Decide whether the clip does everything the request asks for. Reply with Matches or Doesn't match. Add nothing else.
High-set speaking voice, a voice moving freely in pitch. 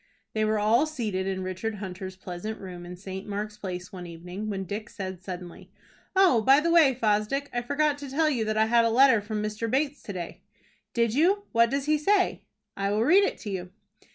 Matches